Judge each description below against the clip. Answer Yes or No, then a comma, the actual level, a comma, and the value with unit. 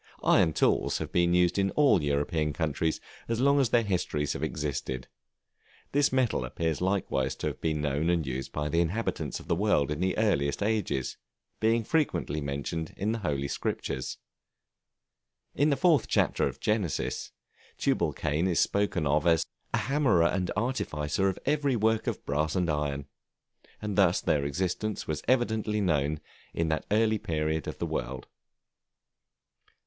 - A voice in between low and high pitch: No, very low, 85 Hz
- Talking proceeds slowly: No, average, 160 wpm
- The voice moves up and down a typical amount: No, wide, 6.5 semitones